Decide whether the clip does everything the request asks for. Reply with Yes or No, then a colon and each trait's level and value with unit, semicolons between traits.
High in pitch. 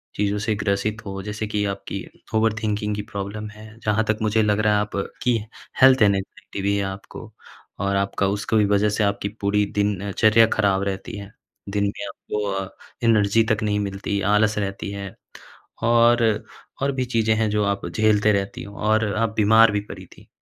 No: low, 105 Hz